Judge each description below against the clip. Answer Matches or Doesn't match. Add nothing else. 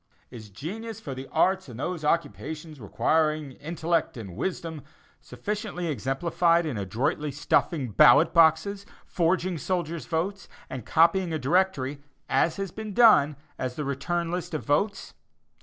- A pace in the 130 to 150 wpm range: Matches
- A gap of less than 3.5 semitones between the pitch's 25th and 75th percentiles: Doesn't match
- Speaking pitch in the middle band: Matches